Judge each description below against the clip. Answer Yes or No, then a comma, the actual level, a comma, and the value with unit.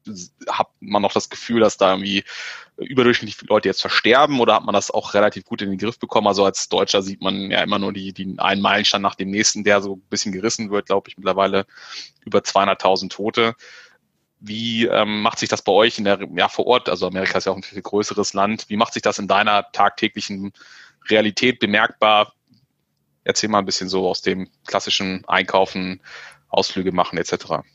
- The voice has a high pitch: No, low, 100 Hz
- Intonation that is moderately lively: No, narrow, 2.1 semitones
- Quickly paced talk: Yes, fast, 200 wpm